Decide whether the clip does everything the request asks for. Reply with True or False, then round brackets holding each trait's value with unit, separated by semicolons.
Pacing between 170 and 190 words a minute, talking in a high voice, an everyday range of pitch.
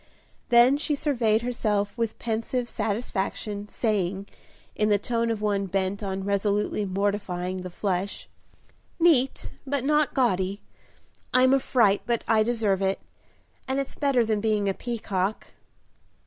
False (135 wpm; 215 Hz; 3.4 semitones)